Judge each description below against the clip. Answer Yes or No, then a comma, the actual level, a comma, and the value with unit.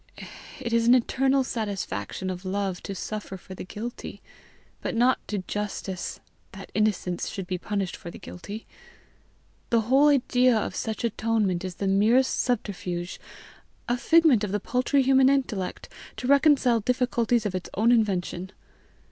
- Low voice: No, high, 220 Hz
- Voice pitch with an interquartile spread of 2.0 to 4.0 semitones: No, average, 4.5 semitones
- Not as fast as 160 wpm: Yes, average, 150 wpm